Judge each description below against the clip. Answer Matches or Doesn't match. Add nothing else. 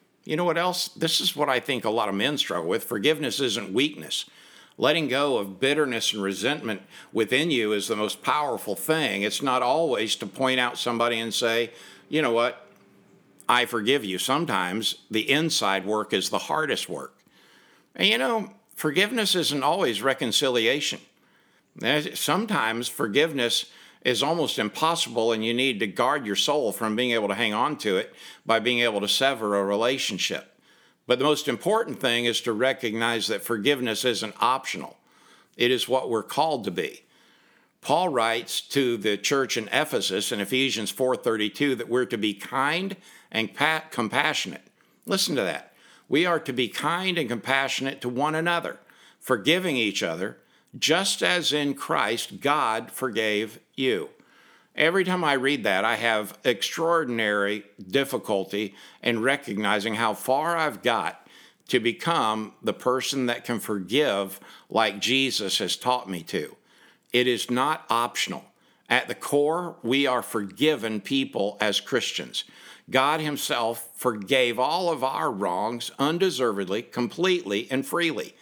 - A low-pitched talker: Matches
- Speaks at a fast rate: Doesn't match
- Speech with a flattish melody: Doesn't match